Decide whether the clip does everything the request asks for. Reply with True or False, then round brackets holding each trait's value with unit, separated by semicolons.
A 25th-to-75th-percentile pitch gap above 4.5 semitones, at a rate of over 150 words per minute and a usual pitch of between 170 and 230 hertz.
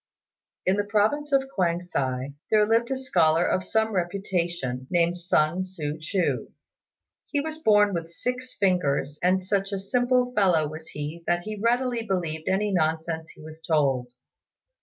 True (5.1 semitones; 160 wpm; 185 Hz)